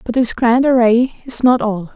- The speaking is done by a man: No, female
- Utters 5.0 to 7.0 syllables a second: No, 4.6 syllables/s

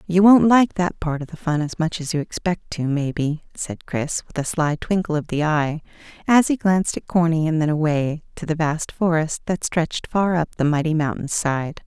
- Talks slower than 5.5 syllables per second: Yes, 5.0 syllables/s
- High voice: No, medium, 160 Hz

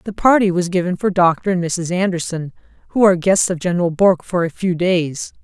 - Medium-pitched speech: Yes, medium, 180 Hz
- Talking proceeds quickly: Yes, fast, 210 wpm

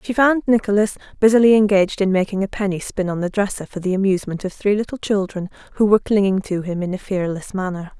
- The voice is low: No, high, 200 Hz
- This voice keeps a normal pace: No, fast, 220 wpm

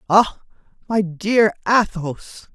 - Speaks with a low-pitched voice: No, high, 200 Hz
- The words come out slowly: Yes, slow, 95 wpm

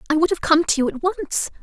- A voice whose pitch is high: Yes, very high, 320 Hz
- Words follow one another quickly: Yes, fast, 295 wpm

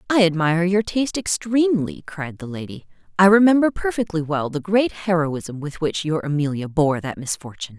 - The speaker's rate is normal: Yes, average, 170 wpm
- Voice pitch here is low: No, medium, 170 Hz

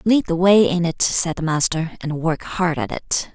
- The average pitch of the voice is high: No, medium, 175 Hz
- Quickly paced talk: Yes, fast, 235 wpm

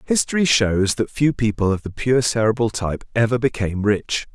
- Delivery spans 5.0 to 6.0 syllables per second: Yes, 5.4 syllables/s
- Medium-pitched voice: No, low, 115 Hz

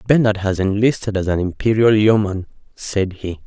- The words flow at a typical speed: Yes, average, 155 wpm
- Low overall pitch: Yes, low, 100 Hz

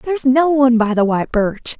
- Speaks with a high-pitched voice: Yes, very high, 250 Hz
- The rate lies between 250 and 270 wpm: No, fast, 235 wpm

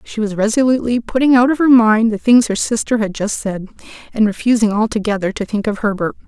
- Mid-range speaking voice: No, high, 220 Hz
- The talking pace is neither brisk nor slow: No, fast, 210 wpm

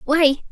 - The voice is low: No, very high, 295 Hz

